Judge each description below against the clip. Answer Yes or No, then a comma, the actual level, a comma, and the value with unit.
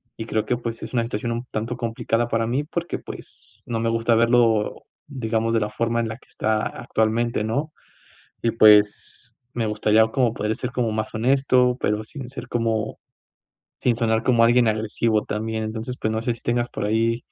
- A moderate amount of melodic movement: No, narrow, 1.6 semitones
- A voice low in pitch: Yes, low, 115 Hz